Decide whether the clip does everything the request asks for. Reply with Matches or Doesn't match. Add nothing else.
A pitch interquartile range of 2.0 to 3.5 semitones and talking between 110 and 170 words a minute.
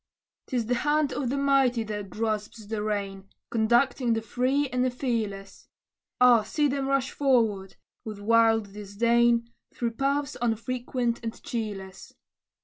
Matches